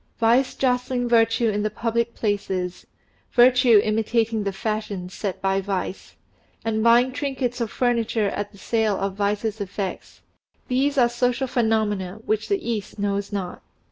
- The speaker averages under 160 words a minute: Yes, average, 145 wpm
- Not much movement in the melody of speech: No, average, 3.1 semitones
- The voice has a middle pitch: No, high, 220 Hz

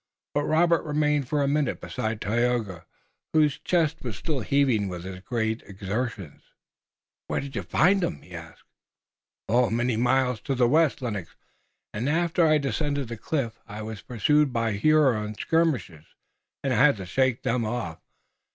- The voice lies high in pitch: No, low, 125 Hz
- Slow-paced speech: No, average, 155 wpm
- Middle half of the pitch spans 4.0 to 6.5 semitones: Yes, wide, 5.4 semitones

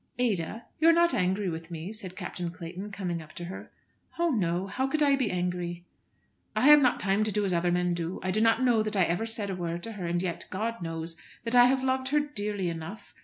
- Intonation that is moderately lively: Yes, average, 5.0 semitones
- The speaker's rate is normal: No, fast, 245 wpm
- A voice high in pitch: Yes, high, 195 Hz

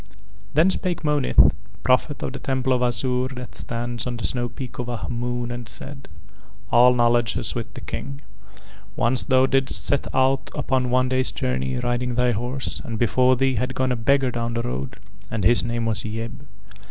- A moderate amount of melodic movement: No, narrow, 1.9 semitones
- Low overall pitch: Yes, low, 125 Hz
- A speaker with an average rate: Yes, average, 190 wpm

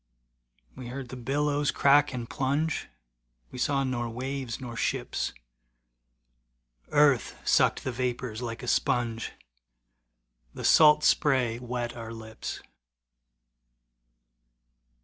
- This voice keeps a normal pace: No, slow, 105 wpm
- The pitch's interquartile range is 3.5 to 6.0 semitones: No, average, 2.7 semitones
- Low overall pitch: Yes, low, 125 Hz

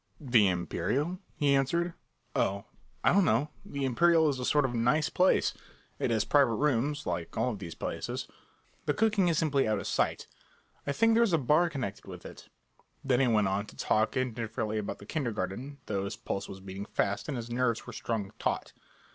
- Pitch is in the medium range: No, low, 125 Hz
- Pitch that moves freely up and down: Yes, wide, 5.9 semitones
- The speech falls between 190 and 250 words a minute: Yes, average, 200 wpm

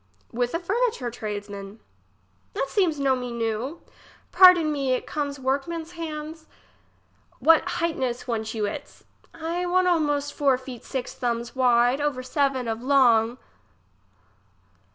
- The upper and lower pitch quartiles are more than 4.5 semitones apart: Yes, average, 4.9 semitones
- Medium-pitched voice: No, very high, 270 Hz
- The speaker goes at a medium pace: No, slow, 130 wpm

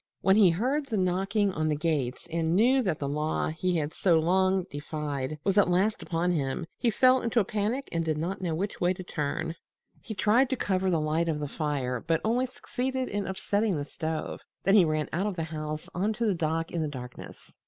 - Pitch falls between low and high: Yes, medium, 175 Hz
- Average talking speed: No, fast, 225 wpm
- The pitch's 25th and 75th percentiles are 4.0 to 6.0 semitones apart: Yes, average, 4.8 semitones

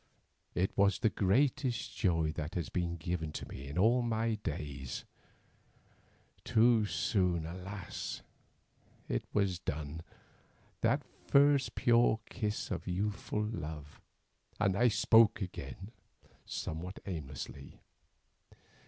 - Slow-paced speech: Yes, slow, 105 wpm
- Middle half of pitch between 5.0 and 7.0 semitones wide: Yes, wide, 5.5 semitones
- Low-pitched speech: Yes, very low, 95 Hz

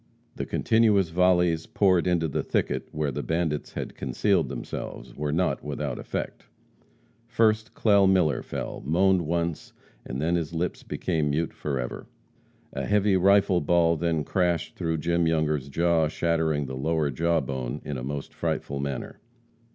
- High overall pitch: No, very low, 80 Hz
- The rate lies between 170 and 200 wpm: No, average, 150 wpm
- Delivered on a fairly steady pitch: No, average, 3.2 semitones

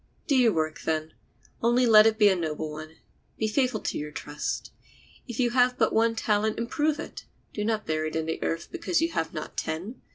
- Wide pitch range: Yes, wide, 7.1 semitones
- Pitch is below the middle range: No, high, 215 Hz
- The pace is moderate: No, fast, 215 wpm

